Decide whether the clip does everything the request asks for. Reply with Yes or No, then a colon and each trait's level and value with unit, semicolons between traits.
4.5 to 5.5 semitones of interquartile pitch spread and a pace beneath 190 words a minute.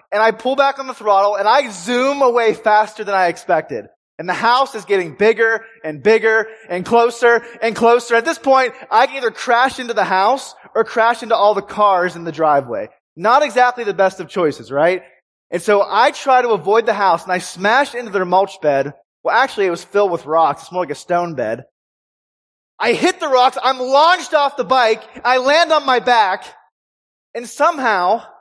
No: average, 5.1 semitones; fast, 205 wpm